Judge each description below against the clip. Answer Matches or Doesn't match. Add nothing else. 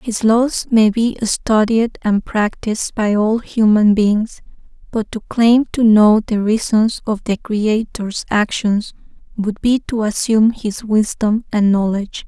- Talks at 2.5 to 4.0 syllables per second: Matches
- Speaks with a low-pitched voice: Doesn't match